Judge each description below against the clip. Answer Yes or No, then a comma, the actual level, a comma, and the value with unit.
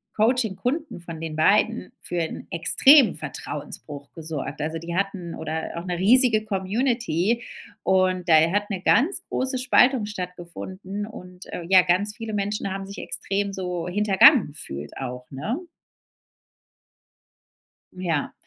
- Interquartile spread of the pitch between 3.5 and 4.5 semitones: Yes, average, 4.1 semitones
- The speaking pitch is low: No, high, 190 Hz